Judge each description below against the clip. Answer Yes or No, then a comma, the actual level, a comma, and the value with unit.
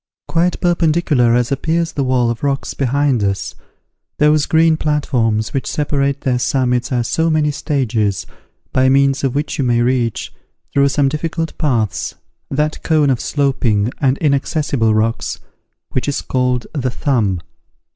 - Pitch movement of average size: Yes, average, 3.6 semitones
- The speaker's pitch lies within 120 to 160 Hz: Yes, low, 135 Hz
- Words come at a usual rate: Yes, average, 145 wpm